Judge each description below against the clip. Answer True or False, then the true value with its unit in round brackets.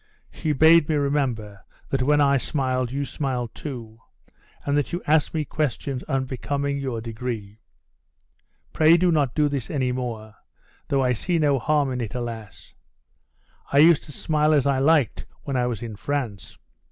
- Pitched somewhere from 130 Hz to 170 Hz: True (135 Hz)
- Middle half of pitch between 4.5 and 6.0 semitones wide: False (3.5 semitones)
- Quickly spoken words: False (165 wpm)